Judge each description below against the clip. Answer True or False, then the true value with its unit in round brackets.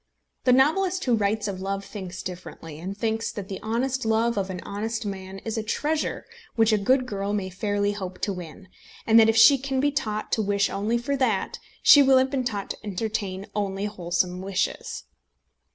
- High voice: True (210 Hz)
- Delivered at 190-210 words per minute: True (200 wpm)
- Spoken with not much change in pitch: False (3.4 semitones)